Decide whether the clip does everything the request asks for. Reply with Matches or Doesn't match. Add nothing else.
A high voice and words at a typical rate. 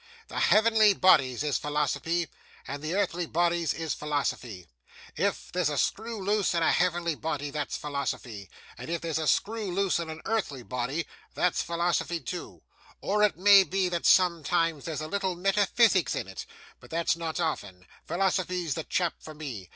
Doesn't match